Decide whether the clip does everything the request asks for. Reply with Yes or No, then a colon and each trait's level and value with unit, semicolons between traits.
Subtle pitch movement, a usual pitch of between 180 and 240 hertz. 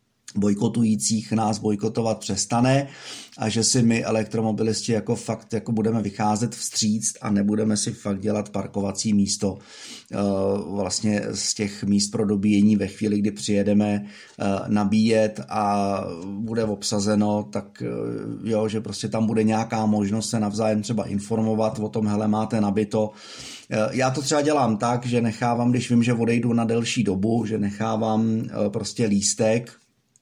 No: narrow, 1.7 semitones; low, 110 Hz